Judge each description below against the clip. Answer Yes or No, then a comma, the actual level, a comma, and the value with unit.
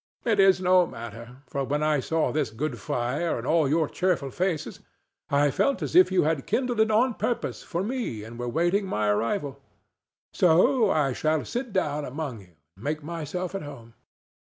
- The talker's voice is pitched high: No, medium, 155 Hz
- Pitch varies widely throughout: Yes, wide, 5.9 semitones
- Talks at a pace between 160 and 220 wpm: Yes, average, 185 wpm